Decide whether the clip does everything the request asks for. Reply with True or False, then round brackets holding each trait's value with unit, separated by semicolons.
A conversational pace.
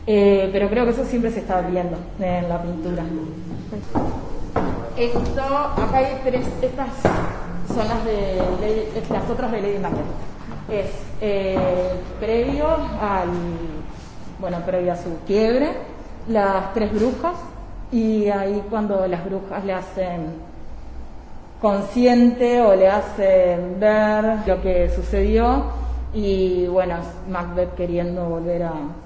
False (120 wpm)